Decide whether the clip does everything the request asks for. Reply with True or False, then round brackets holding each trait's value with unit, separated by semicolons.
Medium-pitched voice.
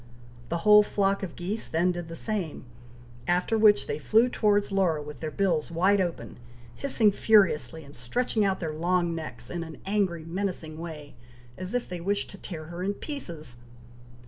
True (180 Hz)